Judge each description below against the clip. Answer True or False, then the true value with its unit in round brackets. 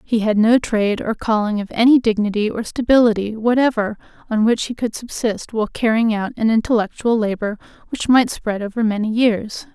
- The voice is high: True (220 Hz)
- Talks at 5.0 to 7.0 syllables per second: True (5.4 syllables/s)